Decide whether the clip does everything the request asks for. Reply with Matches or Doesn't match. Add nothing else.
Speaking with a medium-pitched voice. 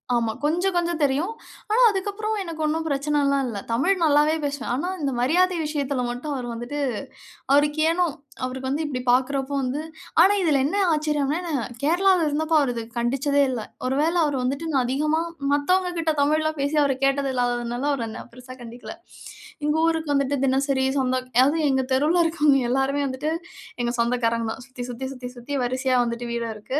Doesn't match